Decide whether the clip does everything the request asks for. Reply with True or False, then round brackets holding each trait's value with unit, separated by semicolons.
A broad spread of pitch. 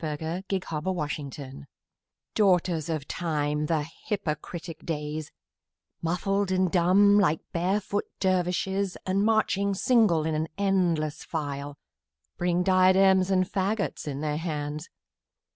False (3.9 semitones)